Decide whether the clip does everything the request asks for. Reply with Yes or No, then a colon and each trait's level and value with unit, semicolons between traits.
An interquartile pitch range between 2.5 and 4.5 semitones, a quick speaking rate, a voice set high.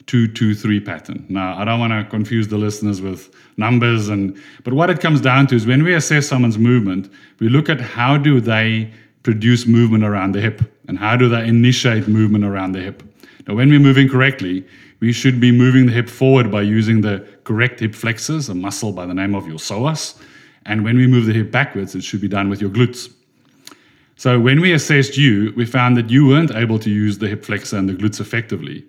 No: average, 3.3 semitones; fast, 220 wpm; low, 115 Hz